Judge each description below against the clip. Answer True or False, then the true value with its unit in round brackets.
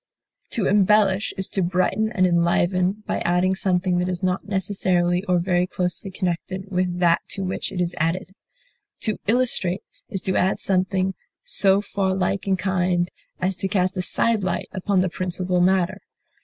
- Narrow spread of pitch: True (1.3 semitones)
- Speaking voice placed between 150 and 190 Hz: True (185 Hz)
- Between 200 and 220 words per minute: False (170 wpm)